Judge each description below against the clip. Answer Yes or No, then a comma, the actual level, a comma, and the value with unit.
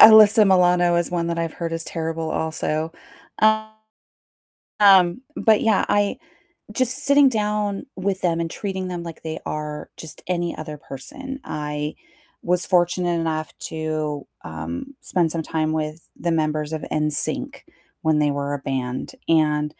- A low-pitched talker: No, medium, 165 Hz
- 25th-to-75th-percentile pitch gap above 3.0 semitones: Yes, average, 3.8 semitones